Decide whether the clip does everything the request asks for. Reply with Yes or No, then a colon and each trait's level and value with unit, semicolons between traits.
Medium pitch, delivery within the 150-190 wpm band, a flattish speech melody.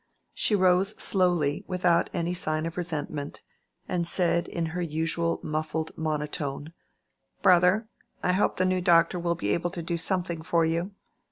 Yes: medium, 170 Hz; average, 155 wpm; narrow, 2.1 semitones